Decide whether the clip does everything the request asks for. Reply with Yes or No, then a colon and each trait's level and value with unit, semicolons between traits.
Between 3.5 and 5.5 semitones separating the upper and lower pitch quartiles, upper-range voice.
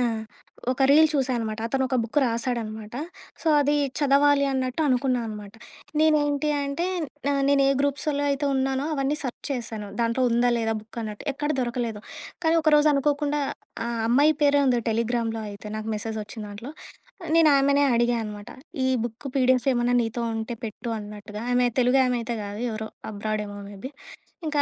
Yes: average, 4.1 semitones; high, 245 Hz